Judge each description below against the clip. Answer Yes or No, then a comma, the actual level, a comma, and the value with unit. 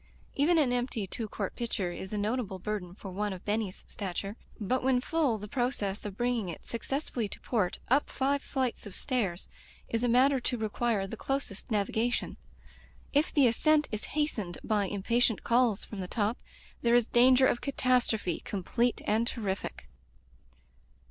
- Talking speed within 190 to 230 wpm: No, average, 165 wpm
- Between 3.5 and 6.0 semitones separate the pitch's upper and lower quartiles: Yes, average, 3.9 semitones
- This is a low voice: No, high, 230 Hz